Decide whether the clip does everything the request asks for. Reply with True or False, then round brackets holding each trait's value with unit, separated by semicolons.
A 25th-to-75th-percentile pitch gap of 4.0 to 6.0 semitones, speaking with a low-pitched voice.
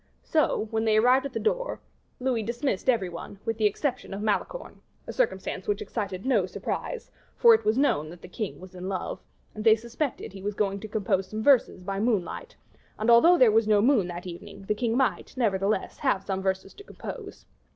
False (4.8 semitones; 215 Hz)